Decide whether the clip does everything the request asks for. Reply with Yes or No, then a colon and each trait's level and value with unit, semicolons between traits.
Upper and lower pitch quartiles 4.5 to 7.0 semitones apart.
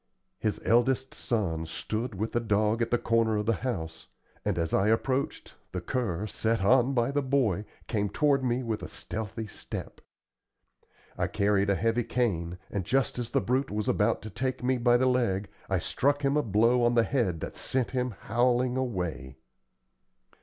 No: average, 3.8 semitones